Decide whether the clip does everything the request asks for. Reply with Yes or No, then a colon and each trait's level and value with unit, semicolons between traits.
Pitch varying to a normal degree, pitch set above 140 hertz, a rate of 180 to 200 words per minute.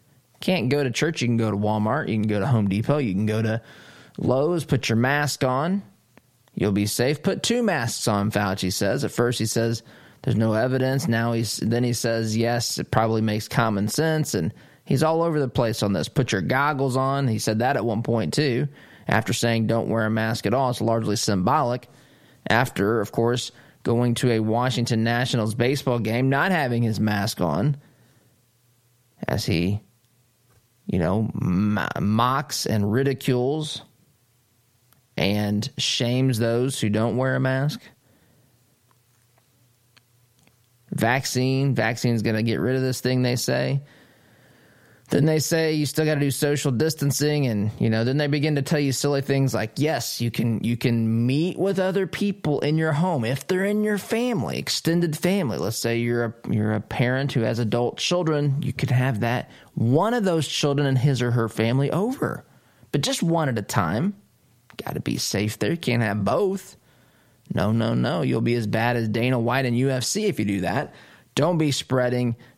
No: average, 3.9 semitones; low, 120 Hz; average, 185 wpm